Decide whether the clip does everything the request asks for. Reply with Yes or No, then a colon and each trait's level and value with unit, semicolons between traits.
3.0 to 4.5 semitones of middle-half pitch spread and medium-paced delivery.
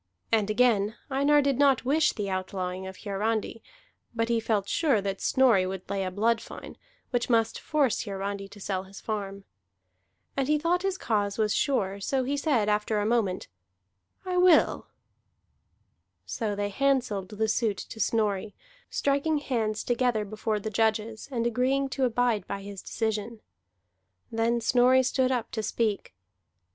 Yes: average, 4.0 semitones; average, 155 wpm